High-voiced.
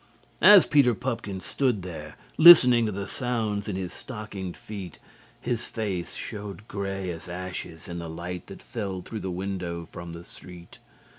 No: very low, 95 Hz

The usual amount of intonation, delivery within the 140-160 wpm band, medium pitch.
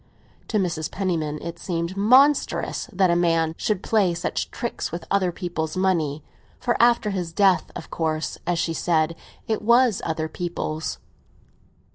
Yes: average, 3.7 semitones; average, 150 wpm; medium, 175 Hz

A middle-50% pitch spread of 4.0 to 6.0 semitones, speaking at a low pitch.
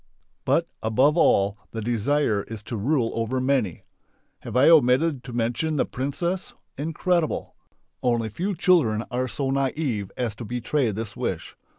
Yes: average, 4.8 semitones; low, 125 Hz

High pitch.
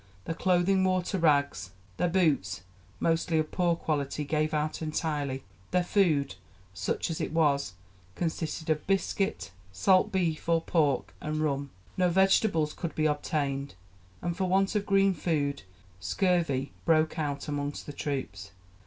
No: medium, 155 Hz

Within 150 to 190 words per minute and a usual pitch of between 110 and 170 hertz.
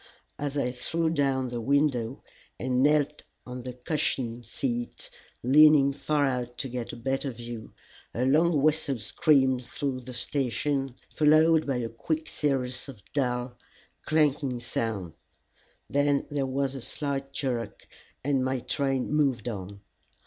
No: average, 140 wpm; low, 135 Hz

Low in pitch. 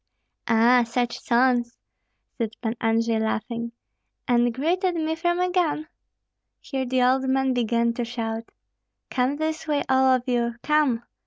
No: very high, 250 Hz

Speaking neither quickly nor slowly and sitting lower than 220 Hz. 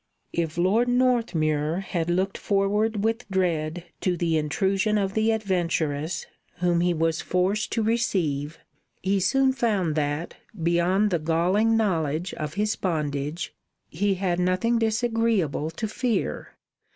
No: slow, 130 wpm; medium, 185 Hz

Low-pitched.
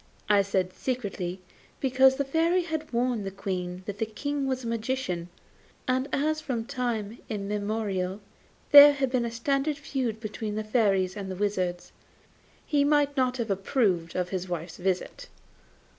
No: high, 225 Hz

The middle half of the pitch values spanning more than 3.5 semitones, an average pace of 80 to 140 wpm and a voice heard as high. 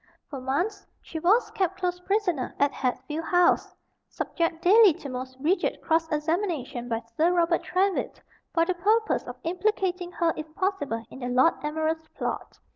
No: average, 4.2 semitones; average, 160 wpm; very high, 330 Hz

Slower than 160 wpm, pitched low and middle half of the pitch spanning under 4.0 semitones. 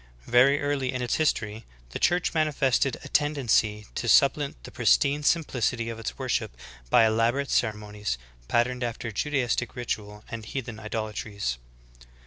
No: average, 140 wpm; low, 120 Hz; average, 4.3 semitones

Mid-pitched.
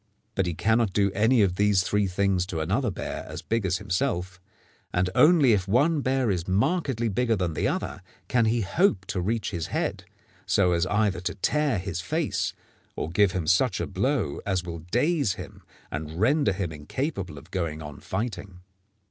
No: low, 100 Hz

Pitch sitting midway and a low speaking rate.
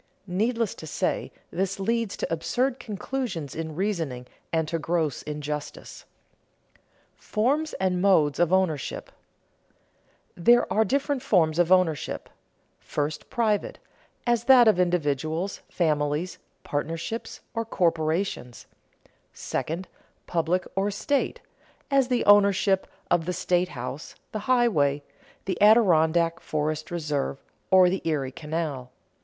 Yes: medium, 175 Hz; slow, 115 wpm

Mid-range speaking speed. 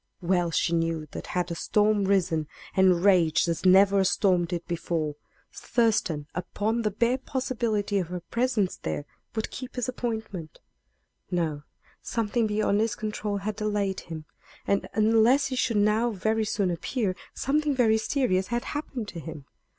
Yes: average, 160 wpm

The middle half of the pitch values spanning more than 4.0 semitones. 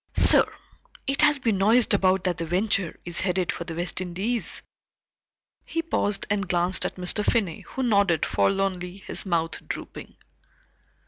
No: average, 3.0 semitones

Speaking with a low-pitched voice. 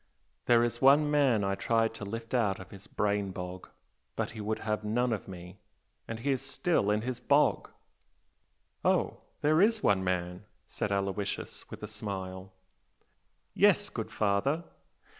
Yes: low, 105 Hz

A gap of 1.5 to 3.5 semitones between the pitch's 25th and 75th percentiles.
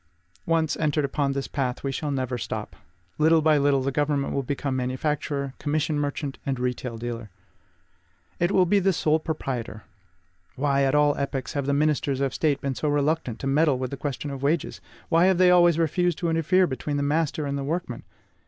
Yes: average, 2.7 semitones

